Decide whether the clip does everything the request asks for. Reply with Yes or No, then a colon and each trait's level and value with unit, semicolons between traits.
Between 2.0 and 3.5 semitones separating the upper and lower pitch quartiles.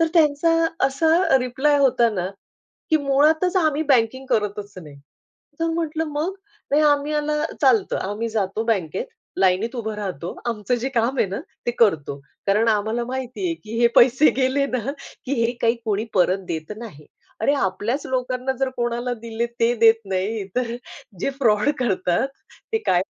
No: average, 4.9 semitones